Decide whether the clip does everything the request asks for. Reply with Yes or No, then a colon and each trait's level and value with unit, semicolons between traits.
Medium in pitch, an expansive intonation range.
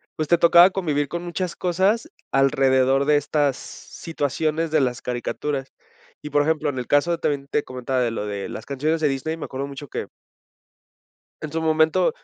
No: medium, 145 Hz; average, 3.2 semitones